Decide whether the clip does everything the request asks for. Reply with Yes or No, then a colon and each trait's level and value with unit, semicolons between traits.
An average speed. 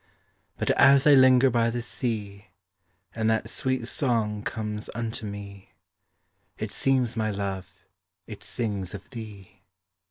No: slow, 130 wpm